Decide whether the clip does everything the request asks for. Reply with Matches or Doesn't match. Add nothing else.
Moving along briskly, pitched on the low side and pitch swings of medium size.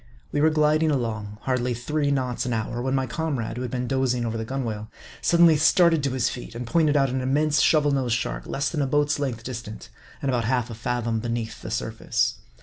Matches